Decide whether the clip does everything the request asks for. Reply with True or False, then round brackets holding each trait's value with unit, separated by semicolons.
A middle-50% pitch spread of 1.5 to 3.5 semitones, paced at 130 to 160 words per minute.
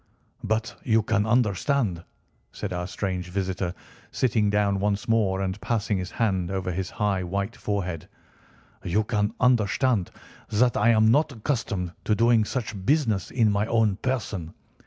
True (3.1 semitones; 150 wpm)